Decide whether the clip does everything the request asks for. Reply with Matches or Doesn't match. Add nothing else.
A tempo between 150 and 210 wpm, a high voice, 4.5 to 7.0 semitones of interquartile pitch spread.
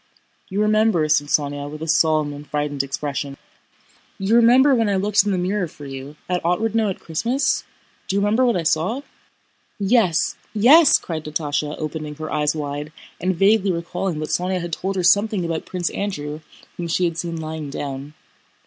Doesn't match